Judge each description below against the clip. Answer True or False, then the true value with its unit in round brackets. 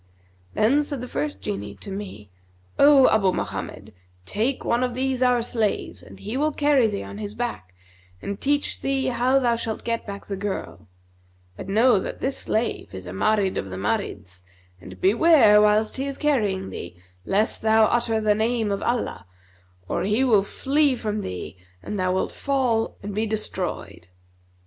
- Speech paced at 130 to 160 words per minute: False (175 wpm)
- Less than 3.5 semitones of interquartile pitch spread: False (4.7 semitones)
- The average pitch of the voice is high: True (215 Hz)